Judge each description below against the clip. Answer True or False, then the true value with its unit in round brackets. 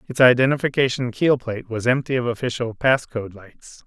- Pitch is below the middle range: True (125 Hz)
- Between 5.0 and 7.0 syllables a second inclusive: True (5.4 syllables/s)